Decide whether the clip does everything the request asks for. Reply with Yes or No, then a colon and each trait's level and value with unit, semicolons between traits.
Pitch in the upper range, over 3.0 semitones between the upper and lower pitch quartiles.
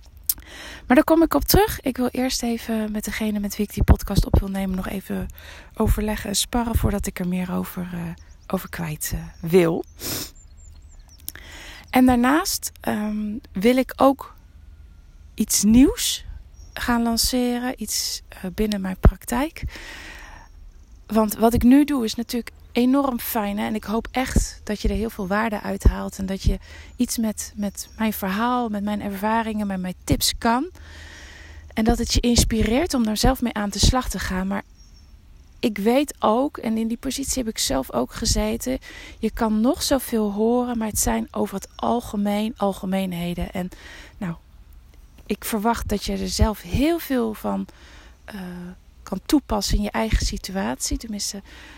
Yes: high, 210 Hz; average, 5.0 semitones